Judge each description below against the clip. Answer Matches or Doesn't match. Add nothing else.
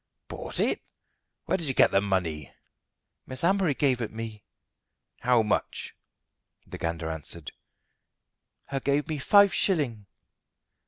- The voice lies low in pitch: Matches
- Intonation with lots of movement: Matches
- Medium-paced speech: Doesn't match